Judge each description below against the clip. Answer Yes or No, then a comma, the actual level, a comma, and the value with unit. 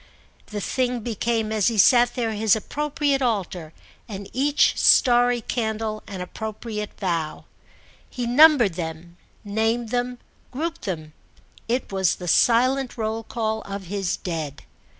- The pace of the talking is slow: Yes, slow, 130 wpm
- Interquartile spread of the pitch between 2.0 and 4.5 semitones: Yes, average, 3.9 semitones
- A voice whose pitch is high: Yes, high, 220 Hz